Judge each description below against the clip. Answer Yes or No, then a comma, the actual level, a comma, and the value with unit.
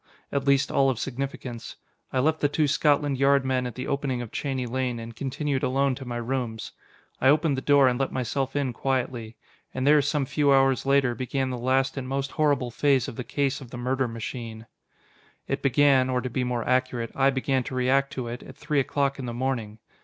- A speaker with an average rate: No, fast, 215 wpm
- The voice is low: Yes, low, 130 Hz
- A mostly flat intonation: Yes, narrow, 1.9 semitones